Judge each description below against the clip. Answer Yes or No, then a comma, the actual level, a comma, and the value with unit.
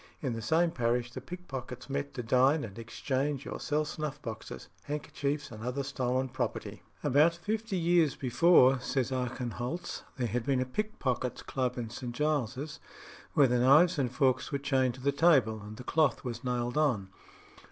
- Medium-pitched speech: No, low, 130 Hz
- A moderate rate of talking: Yes, average, 175 wpm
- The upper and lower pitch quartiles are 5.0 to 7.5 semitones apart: No, average, 3.3 semitones